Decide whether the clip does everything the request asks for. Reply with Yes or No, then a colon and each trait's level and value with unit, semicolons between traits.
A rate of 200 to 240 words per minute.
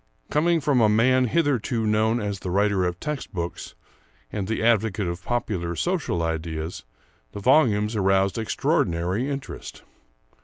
No: average, 140 wpm